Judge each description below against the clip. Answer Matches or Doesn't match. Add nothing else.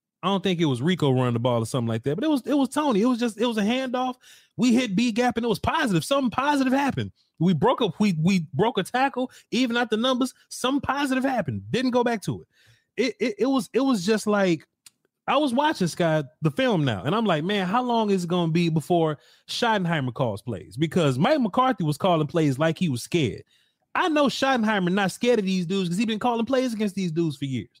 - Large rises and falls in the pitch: Matches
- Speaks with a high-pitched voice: Matches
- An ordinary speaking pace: Doesn't match